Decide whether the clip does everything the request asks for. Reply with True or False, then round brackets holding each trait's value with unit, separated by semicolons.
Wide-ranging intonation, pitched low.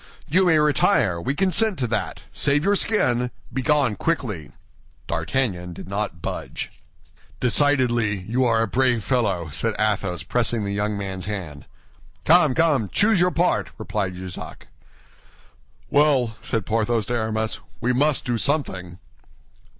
True (6.3 semitones; 120 Hz)